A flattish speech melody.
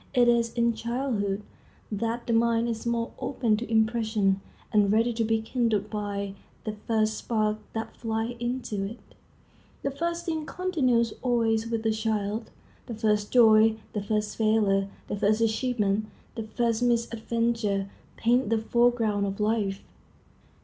Yes: narrow, 1.9 semitones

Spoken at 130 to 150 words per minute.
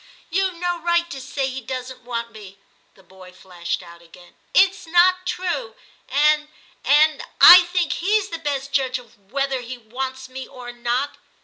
No: average, 190 wpm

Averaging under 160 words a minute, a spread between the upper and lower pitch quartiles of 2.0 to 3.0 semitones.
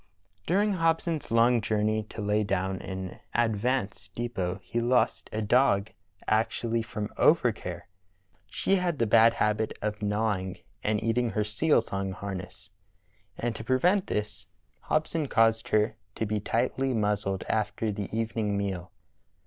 Yes: average, 140 wpm; average, 2.7 semitones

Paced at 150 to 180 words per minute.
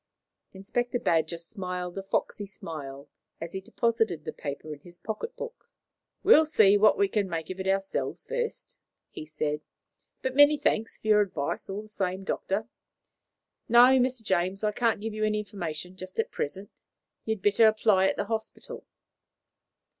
Yes: average, 170 wpm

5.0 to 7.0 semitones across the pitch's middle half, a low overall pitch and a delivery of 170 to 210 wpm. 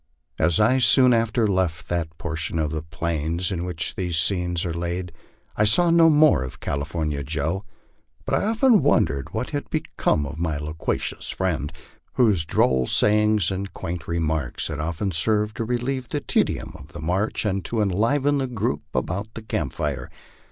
Yes: wide, 5.4 semitones; very low, 90 Hz; average, 175 wpm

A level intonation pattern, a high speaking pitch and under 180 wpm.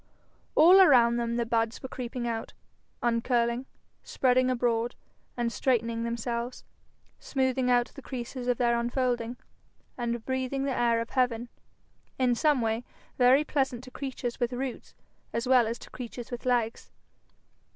Yes: narrow, 1.6 semitones; high, 245 Hz; average, 140 wpm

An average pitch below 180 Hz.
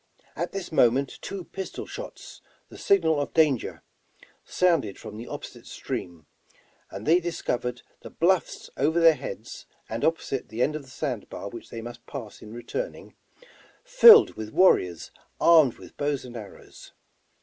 Yes: medium, 140 Hz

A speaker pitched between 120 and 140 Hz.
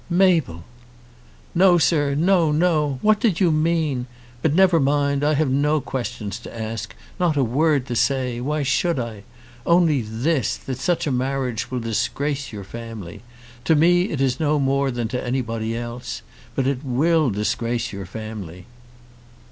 Yes: low, 135 Hz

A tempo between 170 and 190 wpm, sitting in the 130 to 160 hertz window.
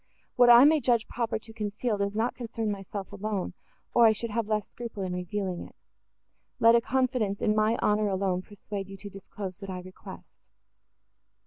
No: average, 185 wpm; high, 210 Hz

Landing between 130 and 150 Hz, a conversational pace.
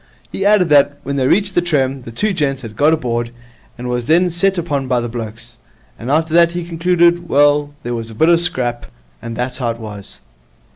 No: medium, 140 Hz; fast, 225 wpm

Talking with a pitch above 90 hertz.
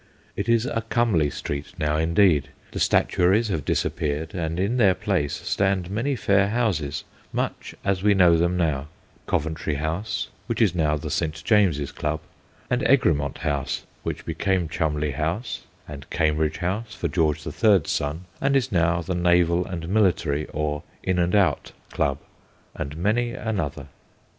No: very low, 85 Hz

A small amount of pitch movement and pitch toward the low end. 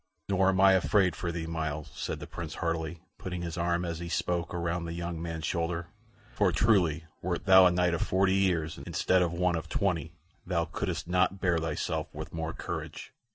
Yes: narrow, 1.7 semitones; very low, 85 Hz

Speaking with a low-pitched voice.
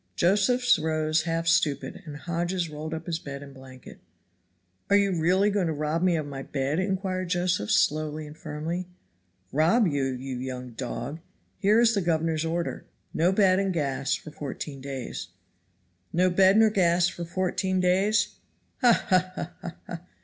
No: medium, 165 Hz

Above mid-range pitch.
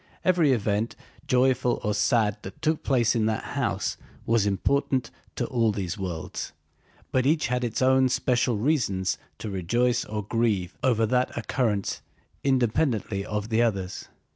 No: low, 115 Hz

